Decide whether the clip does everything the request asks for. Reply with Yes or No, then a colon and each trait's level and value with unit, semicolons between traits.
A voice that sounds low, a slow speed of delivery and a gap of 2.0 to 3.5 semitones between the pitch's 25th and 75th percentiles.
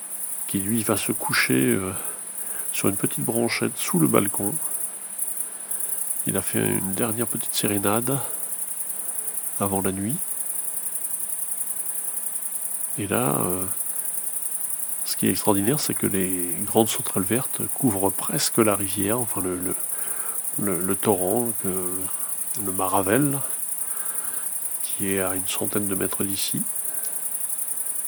Yes: low, 100 Hz; slow, 120 wpm; average, 3.0 semitones